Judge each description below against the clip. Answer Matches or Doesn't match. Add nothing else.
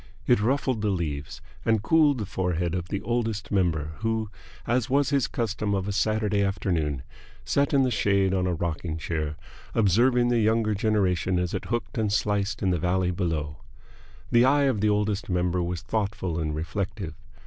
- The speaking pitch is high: Doesn't match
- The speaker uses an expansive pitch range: Doesn't match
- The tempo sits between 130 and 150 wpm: Doesn't match